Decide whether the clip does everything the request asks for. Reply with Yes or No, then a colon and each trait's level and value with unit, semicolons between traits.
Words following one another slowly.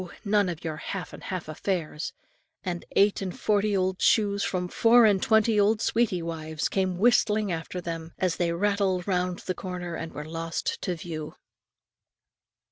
No: average, 165 wpm